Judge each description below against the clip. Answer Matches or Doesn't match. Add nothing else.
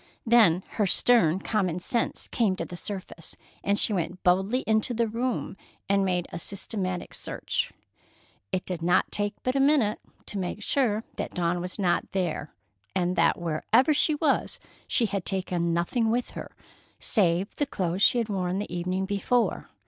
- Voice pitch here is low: Doesn't match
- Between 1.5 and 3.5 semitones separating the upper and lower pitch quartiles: Doesn't match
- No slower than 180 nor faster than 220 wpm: Doesn't match